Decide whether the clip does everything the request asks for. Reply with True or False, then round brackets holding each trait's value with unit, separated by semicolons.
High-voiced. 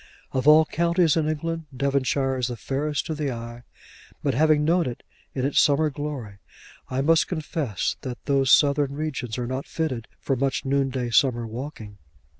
False (140 Hz)